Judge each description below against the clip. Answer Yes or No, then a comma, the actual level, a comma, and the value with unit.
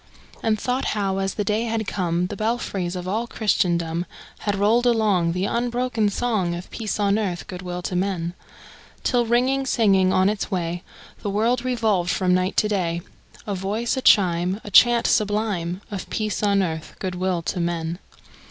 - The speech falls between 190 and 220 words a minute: No, average, 180 wpm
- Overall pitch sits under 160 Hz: No, high, 200 Hz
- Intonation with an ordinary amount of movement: Yes, average, 3.7 semitones